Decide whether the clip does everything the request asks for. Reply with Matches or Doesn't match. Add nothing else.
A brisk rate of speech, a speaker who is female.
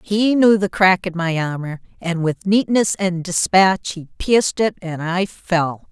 Doesn't match